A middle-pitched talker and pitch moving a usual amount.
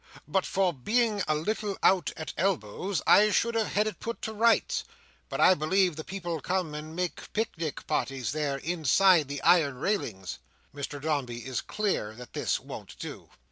No: medium, 170 Hz; wide, 5.7 semitones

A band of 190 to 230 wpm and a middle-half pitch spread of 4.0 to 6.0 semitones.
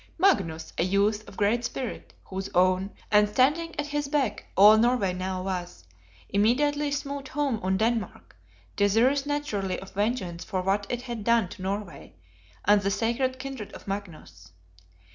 No: average, 155 wpm; average, 5.2 semitones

